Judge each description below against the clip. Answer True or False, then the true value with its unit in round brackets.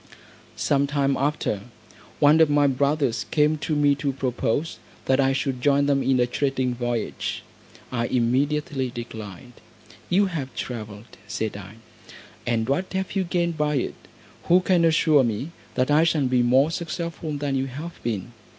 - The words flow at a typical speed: True (160 wpm)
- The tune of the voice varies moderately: True (3.6 semitones)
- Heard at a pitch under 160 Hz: True (140 Hz)